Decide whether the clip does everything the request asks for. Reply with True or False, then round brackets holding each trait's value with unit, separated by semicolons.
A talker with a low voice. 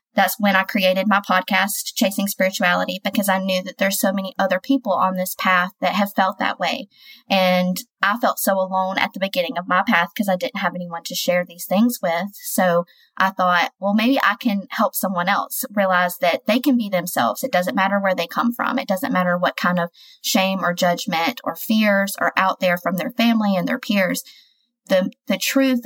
False (195 Hz)